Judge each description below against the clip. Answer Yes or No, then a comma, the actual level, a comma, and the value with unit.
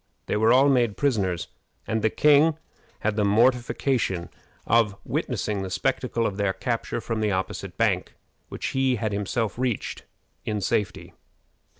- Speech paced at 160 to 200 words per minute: No, average, 150 wpm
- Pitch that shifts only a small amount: No, average, 3.7 semitones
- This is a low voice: Yes, low, 110 Hz